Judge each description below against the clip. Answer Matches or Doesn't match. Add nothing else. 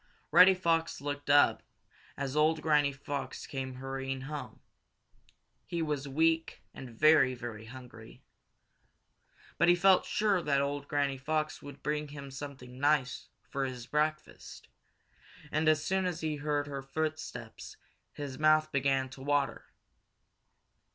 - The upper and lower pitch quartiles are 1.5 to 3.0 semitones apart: Matches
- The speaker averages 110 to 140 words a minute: Matches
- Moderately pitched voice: Matches